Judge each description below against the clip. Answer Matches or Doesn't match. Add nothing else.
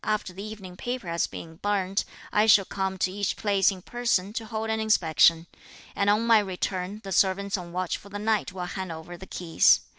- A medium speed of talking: Doesn't match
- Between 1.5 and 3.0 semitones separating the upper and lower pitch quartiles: Matches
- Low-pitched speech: Doesn't match